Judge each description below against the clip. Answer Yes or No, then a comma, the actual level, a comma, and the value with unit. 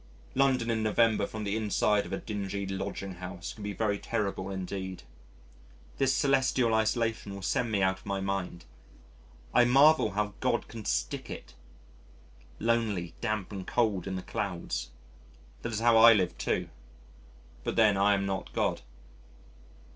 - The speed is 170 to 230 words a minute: No, average, 155 wpm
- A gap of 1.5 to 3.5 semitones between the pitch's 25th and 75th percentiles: Yes, average, 2.8 semitones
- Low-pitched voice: Yes, low, 105 Hz